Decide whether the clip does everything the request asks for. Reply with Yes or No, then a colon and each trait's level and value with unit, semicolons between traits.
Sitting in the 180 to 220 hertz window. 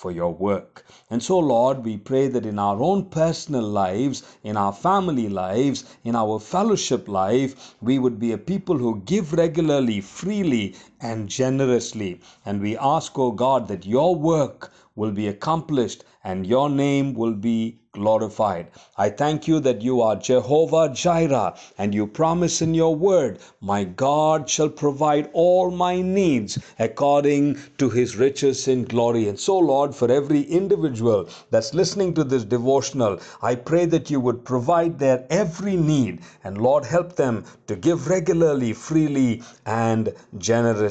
No: low, 130 Hz